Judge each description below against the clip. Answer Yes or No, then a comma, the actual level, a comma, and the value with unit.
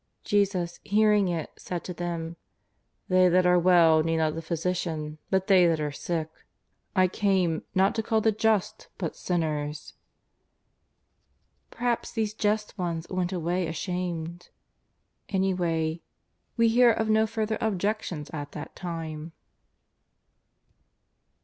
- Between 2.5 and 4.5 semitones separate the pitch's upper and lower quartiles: Yes, average, 3.9 semitones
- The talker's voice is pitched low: No, medium, 180 Hz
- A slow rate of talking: Yes, slow, 130 wpm